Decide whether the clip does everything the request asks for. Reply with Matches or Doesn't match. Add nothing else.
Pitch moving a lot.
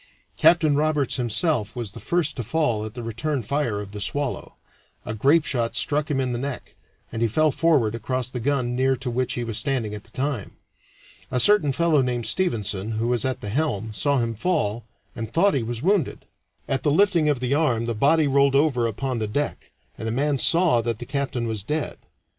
Doesn't match